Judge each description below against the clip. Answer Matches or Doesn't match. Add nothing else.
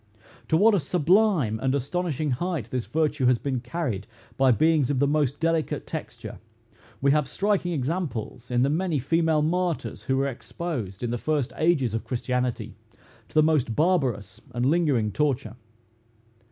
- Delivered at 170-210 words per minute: Doesn't match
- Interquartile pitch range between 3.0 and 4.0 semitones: Doesn't match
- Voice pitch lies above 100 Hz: Matches